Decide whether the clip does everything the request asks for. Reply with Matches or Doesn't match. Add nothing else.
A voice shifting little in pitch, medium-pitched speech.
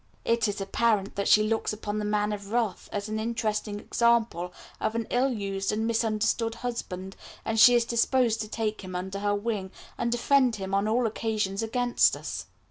Doesn't match